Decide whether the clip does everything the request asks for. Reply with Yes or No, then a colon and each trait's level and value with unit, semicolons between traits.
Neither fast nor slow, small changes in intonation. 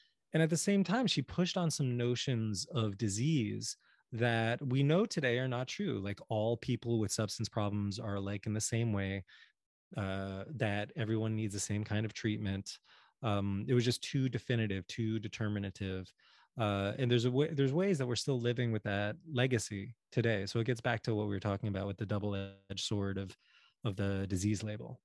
No: average, 195 wpm; average, 3.5 semitones